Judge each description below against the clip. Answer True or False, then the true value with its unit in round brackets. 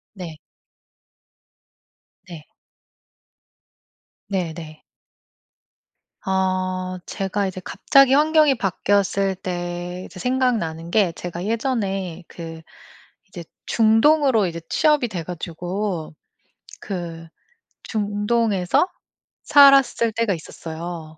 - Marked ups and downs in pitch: False (4.5 semitones)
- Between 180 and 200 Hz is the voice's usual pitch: True (190 Hz)